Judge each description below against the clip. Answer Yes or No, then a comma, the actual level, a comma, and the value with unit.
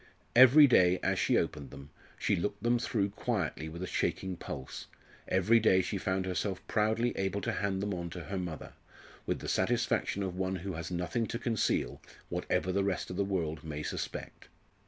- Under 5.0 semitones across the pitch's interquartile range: Yes, average, 2.8 semitones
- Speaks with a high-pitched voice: No, very low, 95 Hz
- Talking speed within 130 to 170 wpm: No, average, 190 wpm